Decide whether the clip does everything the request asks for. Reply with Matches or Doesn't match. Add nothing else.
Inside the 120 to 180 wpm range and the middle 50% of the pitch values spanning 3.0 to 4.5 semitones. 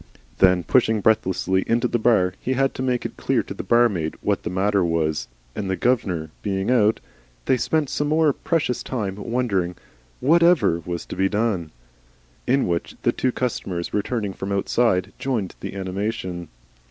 Doesn't match